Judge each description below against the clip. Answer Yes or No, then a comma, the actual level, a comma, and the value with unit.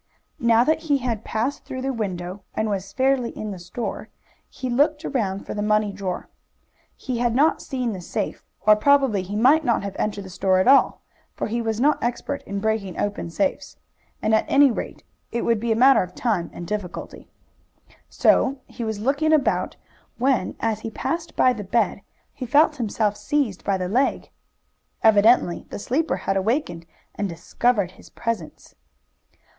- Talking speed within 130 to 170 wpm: No, average, 180 wpm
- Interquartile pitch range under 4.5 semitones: No, average, 4.8 semitones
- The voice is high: Yes, high, 225 Hz